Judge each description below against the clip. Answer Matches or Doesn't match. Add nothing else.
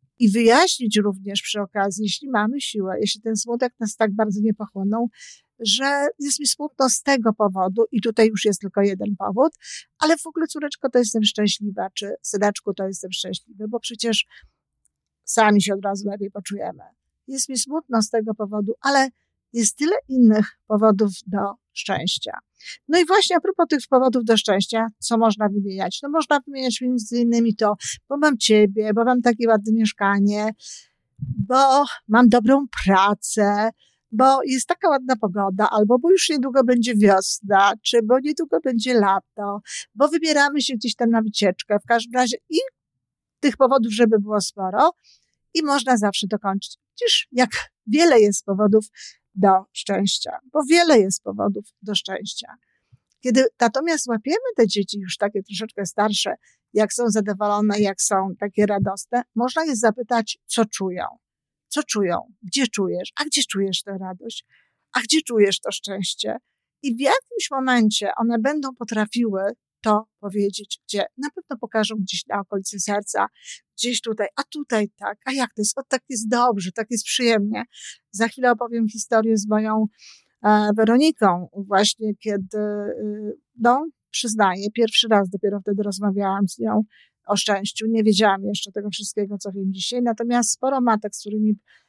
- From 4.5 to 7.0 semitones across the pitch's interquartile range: Doesn't match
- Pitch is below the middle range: Doesn't match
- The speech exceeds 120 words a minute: Matches